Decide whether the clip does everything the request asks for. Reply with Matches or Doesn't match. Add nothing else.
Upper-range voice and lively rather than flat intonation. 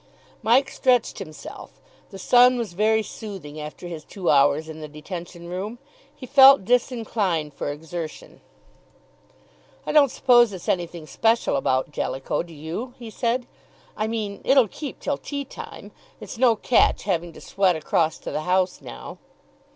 Matches